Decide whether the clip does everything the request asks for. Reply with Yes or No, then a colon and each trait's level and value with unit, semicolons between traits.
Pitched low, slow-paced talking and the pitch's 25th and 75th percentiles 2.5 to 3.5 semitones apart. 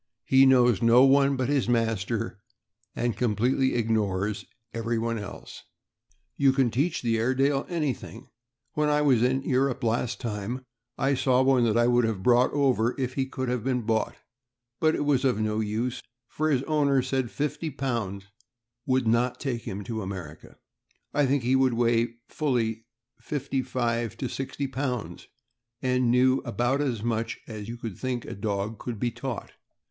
No: low, 125 Hz; average, 170 wpm; average, 2.8 semitones